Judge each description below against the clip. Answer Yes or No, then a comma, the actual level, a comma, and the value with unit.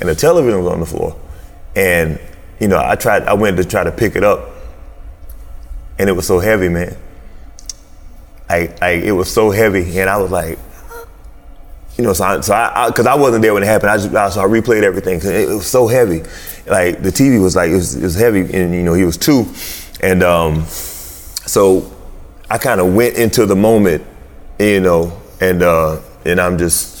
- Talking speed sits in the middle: No, fast, 215 wpm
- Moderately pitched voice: No, very low, 90 Hz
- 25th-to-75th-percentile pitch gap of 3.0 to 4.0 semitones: Yes, average, 3.4 semitones